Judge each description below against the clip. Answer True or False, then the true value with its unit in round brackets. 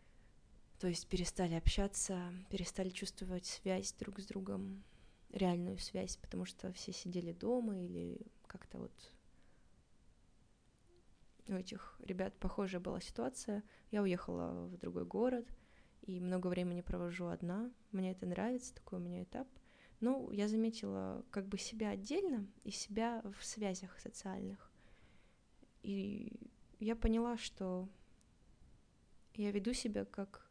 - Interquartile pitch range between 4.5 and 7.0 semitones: False (3.5 semitones)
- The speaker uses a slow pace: False (125 wpm)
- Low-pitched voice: False (190 Hz)